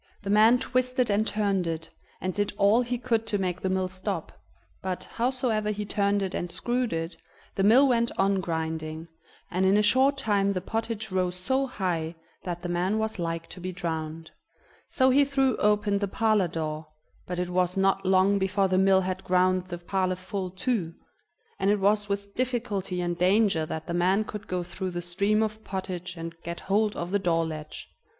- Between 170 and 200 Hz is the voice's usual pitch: Yes, high, 190 Hz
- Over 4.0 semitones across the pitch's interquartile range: No, average, 3.2 semitones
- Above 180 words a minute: Yes, average, 195 wpm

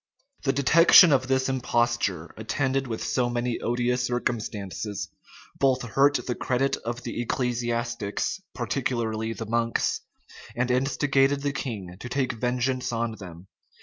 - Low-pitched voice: Yes, low, 120 Hz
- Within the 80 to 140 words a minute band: Yes, slow, 135 wpm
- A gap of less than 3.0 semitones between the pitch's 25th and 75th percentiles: Yes, narrow, 2.5 semitones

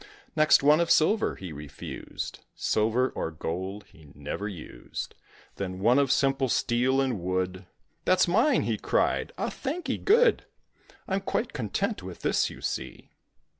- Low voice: Yes, low, 125 Hz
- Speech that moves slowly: No, average, 145 wpm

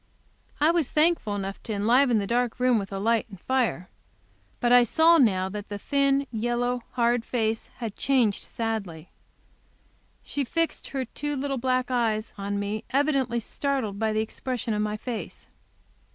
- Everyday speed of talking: Yes, average, 160 wpm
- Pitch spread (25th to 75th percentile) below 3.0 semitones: No, average, 3.8 semitones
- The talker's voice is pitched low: No, high, 235 Hz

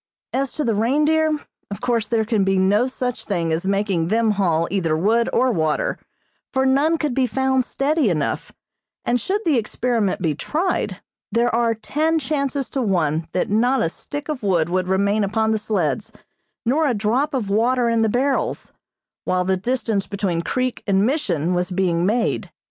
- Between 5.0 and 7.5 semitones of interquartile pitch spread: Yes, wide, 5.4 semitones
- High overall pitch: Yes, high, 220 Hz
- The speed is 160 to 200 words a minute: Yes, average, 180 wpm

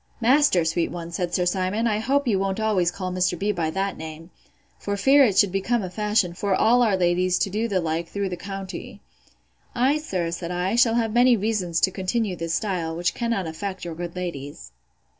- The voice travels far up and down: No, average, 3.8 semitones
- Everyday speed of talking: No, fast, 210 wpm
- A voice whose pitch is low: No, high, 190 Hz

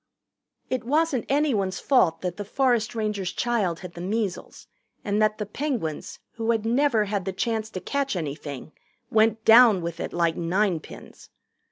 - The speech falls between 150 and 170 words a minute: Yes, average, 160 wpm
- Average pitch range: Yes, average, 4.7 semitones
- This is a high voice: Yes, high, 215 Hz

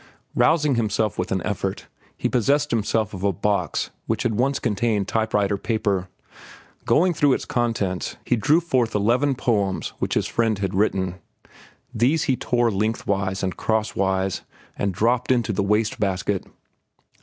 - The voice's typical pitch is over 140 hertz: No, low, 105 Hz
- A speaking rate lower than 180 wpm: Yes, average, 155 wpm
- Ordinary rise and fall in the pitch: Yes, average, 3.6 semitones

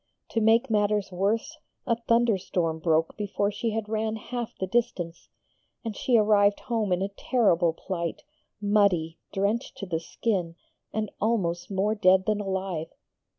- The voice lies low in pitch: No, high, 205 Hz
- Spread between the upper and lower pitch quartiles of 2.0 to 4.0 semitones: Yes, average, 3.5 semitones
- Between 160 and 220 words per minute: No, average, 150 wpm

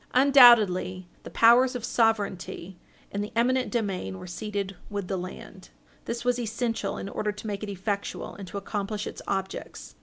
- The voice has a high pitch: Yes, high, 205 Hz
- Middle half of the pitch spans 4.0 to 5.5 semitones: No, average, 3.3 semitones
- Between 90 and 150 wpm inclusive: No, average, 170 wpm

